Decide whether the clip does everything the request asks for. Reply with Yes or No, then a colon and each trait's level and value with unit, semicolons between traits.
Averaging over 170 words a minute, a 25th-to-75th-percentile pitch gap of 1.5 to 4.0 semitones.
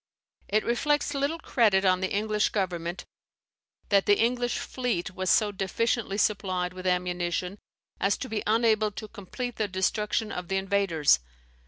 No: average, 150 wpm; average, 3.3 semitones